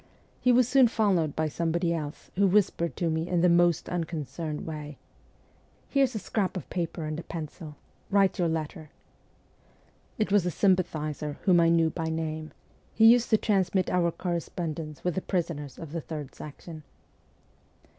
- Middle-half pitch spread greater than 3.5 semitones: No, average, 3.0 semitones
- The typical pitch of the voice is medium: Yes, medium, 170 Hz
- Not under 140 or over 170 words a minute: Yes, average, 165 wpm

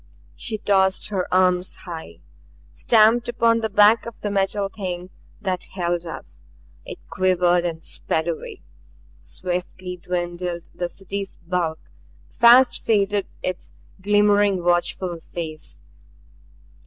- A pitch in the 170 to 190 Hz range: Yes, medium, 185 Hz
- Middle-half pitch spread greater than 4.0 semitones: No, average, 2.8 semitones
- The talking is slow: Yes, slow, 115 wpm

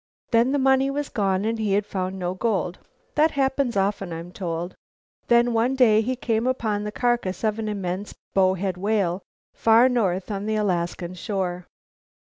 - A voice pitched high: Yes, high, 210 Hz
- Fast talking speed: No, average, 170 wpm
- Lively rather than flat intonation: No, average, 4.2 semitones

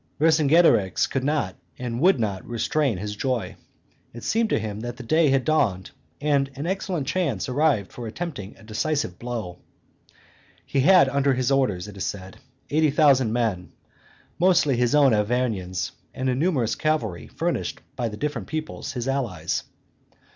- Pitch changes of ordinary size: No, wide, 5.7 semitones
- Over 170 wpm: No, average, 160 wpm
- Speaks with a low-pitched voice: Yes, low, 130 Hz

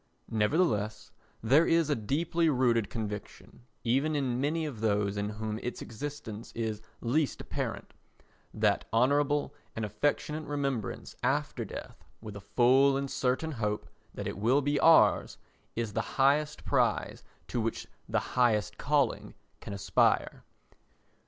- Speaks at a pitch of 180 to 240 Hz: No, low, 125 Hz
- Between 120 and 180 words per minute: Yes, slow, 135 wpm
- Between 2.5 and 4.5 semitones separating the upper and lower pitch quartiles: No, average, 5.2 semitones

